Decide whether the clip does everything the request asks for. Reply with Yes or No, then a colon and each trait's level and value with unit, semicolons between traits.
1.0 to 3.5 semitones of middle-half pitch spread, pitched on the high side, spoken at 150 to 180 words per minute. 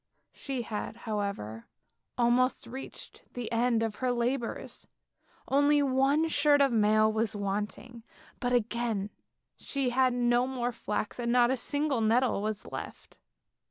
No: average, 3.0 semitones; high, 240 Hz; slow, 135 wpm